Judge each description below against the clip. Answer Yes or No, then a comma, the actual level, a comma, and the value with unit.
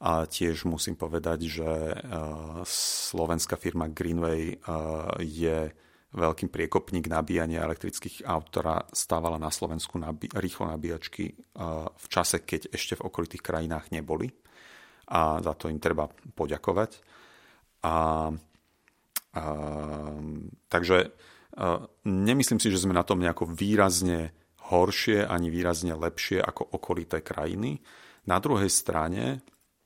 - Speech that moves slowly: No, average, 120 wpm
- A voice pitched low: Yes, very low, 80 Hz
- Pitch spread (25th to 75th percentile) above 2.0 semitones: No, narrow, 1.7 semitones